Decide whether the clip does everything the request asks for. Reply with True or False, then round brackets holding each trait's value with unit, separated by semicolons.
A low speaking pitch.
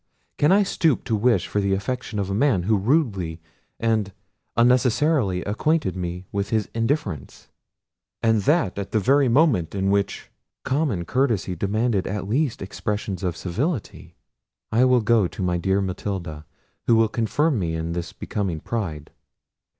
True (105 Hz)